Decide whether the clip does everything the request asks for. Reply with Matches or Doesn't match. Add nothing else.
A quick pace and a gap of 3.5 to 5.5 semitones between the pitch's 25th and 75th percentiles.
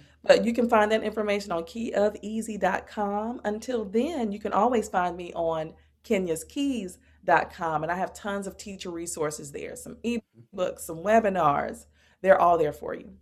Doesn't match